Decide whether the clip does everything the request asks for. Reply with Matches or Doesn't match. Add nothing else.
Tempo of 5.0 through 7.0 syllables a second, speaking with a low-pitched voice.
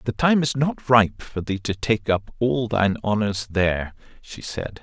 Doesn't match